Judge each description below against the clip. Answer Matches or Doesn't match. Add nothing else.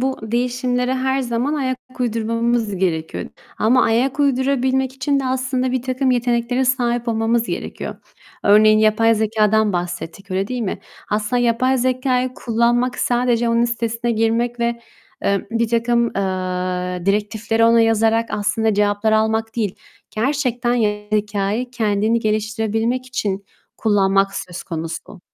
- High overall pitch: Matches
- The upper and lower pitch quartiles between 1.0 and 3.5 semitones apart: Matches